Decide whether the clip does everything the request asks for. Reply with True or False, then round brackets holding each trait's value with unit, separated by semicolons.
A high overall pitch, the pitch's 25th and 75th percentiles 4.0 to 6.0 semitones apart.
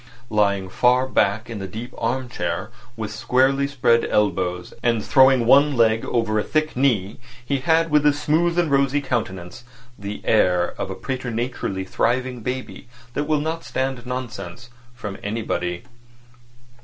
False (120 Hz; 4.4 semitones)